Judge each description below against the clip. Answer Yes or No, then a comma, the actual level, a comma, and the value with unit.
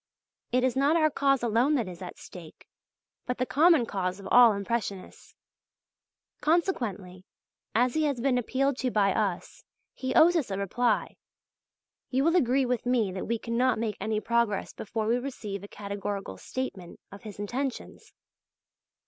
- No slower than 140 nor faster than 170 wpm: Yes, average, 160 wpm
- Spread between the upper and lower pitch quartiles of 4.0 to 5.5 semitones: Yes, average, 4.5 semitones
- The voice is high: Yes, high, 235 Hz